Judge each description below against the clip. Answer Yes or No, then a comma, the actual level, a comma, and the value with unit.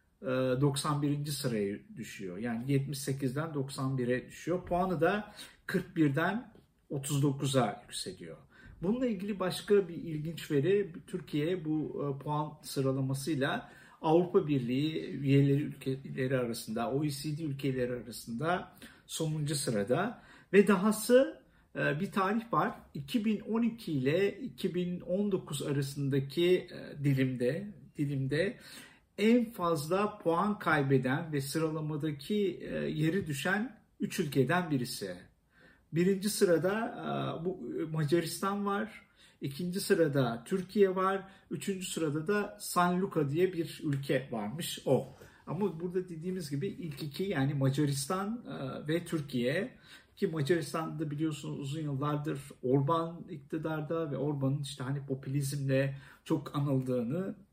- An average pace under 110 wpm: Yes, average, 100 wpm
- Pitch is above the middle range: No, medium, 160 Hz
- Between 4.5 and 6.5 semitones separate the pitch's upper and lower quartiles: Yes, average, 5.2 semitones